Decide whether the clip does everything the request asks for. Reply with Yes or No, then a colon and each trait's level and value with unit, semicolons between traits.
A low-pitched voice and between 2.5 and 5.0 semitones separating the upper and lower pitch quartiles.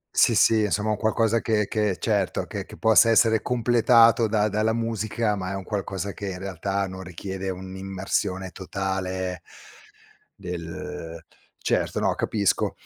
Yes: low, 100 Hz; average, 2.8 semitones